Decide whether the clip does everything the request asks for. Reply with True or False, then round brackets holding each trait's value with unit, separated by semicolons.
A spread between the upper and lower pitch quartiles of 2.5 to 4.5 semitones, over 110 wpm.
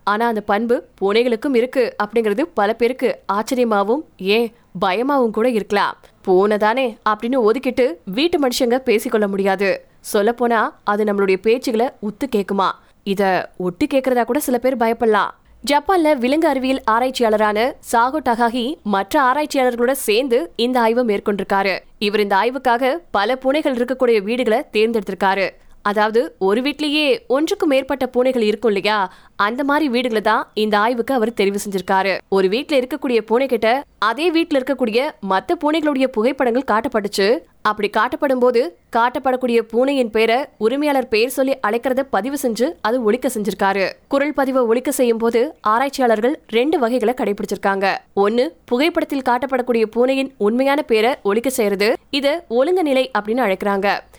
True (3.8 semitones; 130 wpm)